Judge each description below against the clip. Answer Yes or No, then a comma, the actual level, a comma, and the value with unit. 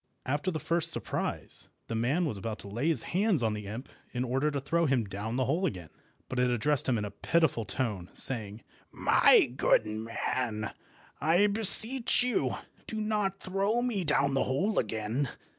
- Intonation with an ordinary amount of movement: No, wide, 7.6 semitones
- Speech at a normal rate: Yes, average, 180 wpm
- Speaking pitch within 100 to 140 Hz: Yes, low, 135 Hz